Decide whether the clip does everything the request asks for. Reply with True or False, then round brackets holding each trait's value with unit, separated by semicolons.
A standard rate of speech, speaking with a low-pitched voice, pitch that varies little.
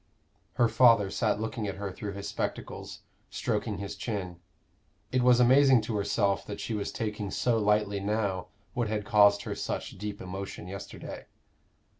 True (160 wpm; 105 Hz; 2.2 semitones)